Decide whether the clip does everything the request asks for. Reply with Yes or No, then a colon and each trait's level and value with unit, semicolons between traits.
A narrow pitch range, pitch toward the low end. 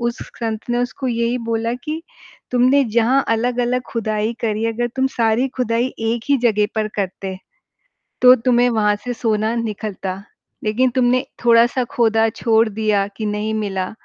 No: narrow, 2.2 semitones; high, 230 Hz